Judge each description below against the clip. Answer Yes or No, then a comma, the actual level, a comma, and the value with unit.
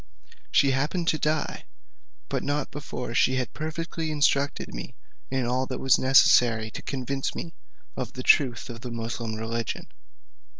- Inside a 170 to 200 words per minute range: No, average, 155 wpm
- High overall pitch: No, low, 130 Hz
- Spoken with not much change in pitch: No, average, 3.7 semitones